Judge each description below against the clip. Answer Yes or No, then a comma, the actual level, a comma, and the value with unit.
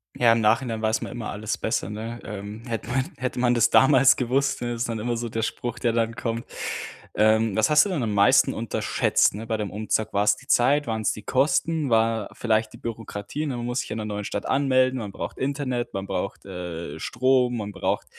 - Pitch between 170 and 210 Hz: No, low, 115 Hz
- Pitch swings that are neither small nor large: Yes, average, 3.0 semitones